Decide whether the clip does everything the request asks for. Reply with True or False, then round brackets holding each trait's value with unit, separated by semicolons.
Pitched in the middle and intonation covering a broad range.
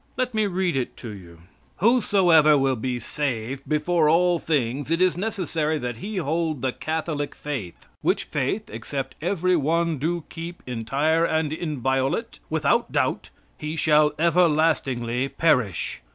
False (155 Hz; 4.3 semitones)